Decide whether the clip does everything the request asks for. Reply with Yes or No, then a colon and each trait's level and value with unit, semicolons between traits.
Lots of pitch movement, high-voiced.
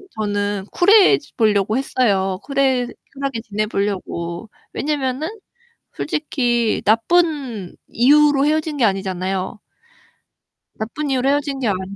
Yes: wide, 5.8 semitones; high, 240 Hz